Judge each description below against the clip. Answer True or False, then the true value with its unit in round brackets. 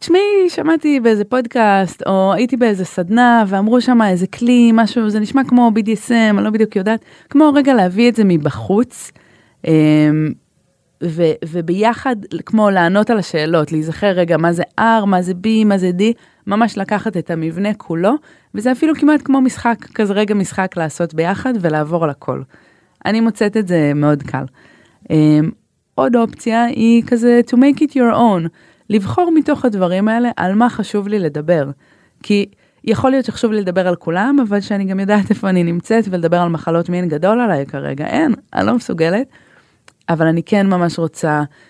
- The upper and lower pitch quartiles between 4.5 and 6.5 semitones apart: True (5.4 semitones)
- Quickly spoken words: True (170 wpm)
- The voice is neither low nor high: False (210 Hz)